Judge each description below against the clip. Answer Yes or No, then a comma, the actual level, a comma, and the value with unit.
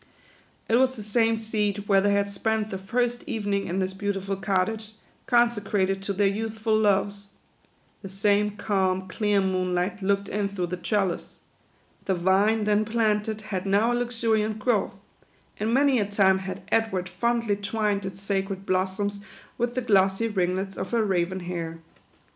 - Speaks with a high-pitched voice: Yes, high, 205 Hz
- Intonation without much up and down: Yes, narrow, 2.3 semitones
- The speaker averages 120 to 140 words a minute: No, average, 160 wpm